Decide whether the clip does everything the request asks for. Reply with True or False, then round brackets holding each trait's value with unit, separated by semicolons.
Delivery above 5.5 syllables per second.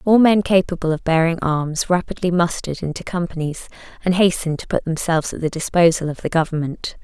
True (6.0 syllables/s)